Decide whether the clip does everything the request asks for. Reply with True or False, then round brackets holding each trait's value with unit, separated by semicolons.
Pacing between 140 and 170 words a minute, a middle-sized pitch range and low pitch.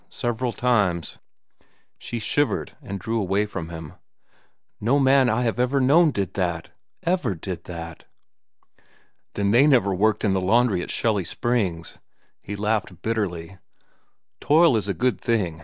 True (150 wpm; 4.9 semitones; 105 Hz)